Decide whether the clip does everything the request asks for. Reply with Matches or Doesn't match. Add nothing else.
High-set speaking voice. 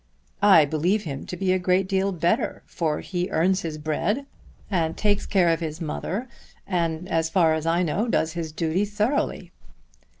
Doesn't match